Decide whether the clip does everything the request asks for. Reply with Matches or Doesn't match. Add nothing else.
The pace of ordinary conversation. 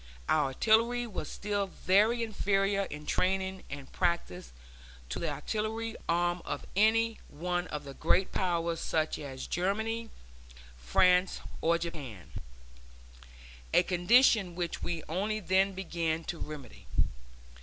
Doesn't match